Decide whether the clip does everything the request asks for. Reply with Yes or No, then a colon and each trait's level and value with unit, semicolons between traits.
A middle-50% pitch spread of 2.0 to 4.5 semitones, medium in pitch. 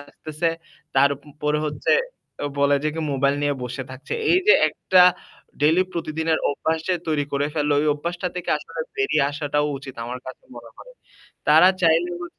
Yes: average, 2.7 semitones; medium, 150 Hz